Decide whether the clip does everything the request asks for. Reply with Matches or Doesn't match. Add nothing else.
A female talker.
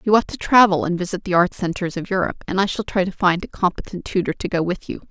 Matches